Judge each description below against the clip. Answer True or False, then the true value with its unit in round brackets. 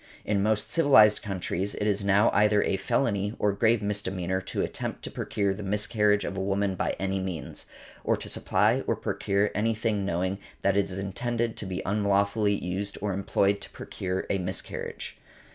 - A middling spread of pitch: False (1.5 semitones)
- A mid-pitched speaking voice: False (100 Hz)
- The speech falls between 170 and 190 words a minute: True (180 wpm)